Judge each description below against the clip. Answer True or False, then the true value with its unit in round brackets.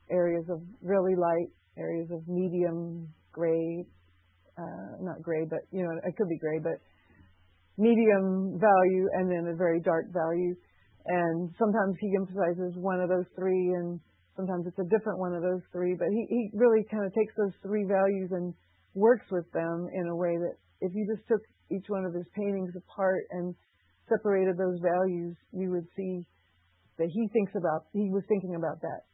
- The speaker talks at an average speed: True (180 wpm)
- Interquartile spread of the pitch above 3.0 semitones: False (2.4 semitones)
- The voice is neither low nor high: True (180 Hz)